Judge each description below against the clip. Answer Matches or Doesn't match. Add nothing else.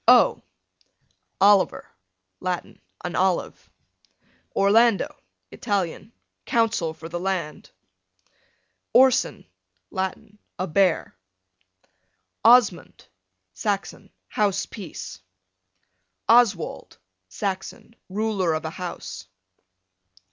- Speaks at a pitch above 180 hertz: Matches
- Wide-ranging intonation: Doesn't match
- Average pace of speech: Doesn't match